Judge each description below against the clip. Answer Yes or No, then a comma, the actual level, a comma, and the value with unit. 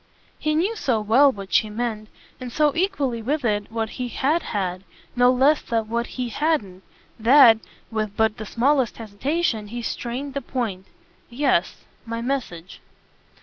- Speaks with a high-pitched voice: Yes, high, 235 Hz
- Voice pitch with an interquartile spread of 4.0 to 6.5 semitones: Yes, average, 4.4 semitones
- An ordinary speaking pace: Yes, average, 155 wpm